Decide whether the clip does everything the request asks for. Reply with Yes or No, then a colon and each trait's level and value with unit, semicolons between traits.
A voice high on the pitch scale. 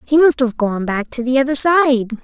Yes: very high, 260 Hz